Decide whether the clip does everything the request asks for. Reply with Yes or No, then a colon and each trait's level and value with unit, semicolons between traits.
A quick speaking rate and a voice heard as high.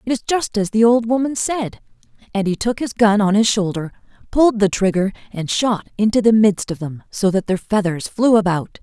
Yes: fast, 215 wpm; high, 210 Hz